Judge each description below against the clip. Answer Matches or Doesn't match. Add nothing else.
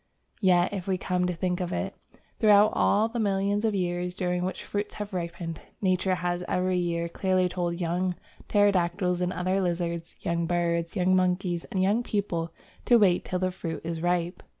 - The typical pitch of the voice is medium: Matches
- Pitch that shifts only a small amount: Matches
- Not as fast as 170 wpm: Doesn't match